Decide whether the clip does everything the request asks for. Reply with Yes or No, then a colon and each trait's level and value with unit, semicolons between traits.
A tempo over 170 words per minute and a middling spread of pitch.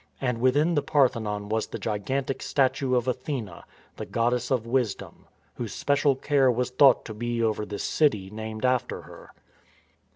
No: average, 165 wpm; average, 3.4 semitones